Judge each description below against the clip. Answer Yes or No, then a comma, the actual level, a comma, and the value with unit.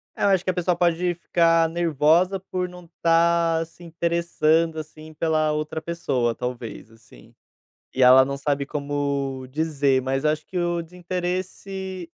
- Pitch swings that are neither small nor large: Yes, average, 3.4 semitones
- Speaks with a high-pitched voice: No, medium, 165 Hz